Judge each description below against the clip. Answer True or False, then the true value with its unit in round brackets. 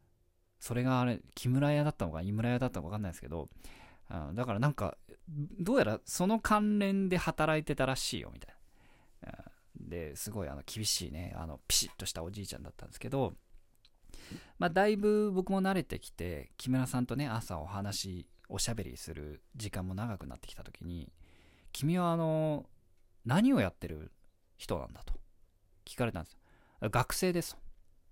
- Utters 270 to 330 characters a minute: False (345 characters per minute)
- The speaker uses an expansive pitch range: True (7.7 semitones)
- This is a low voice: True (100 Hz)